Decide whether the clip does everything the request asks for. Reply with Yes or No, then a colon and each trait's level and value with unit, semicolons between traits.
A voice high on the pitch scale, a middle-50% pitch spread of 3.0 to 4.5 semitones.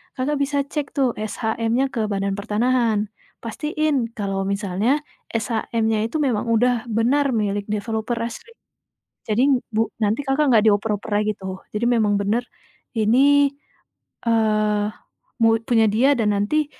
Yes: high, 225 Hz; average, 3.4 semitones